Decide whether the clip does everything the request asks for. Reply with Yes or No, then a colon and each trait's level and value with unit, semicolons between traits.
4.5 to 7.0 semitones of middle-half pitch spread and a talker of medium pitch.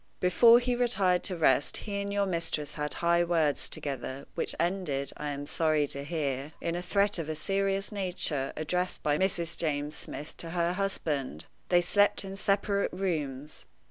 Yes: average, 4.8 semitones; medium, 170 Hz